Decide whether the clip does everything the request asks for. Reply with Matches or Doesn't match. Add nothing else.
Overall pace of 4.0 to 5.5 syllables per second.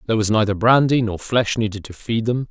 Doesn't match